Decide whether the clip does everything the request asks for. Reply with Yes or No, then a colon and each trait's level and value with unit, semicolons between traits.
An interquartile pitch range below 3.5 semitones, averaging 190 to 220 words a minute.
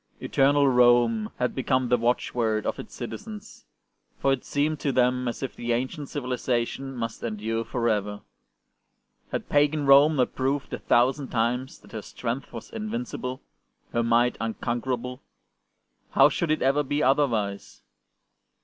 No: average, 2.9 semitones; average, 155 wpm